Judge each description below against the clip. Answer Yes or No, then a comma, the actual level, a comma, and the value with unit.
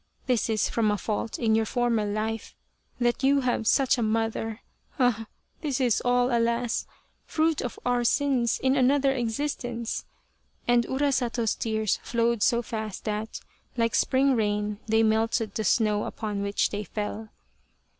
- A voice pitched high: Yes, high, 230 Hz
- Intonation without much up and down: Yes, narrow, 2.3 semitones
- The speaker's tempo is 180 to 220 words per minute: No, average, 150 wpm